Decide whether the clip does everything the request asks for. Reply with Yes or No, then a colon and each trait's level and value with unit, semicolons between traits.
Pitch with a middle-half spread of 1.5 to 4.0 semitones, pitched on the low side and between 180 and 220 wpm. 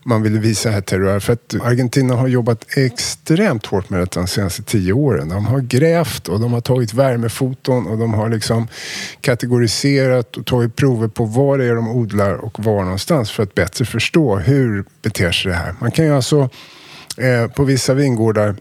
Yes: average, 3.6 semitones; low, 120 Hz; average, 190 wpm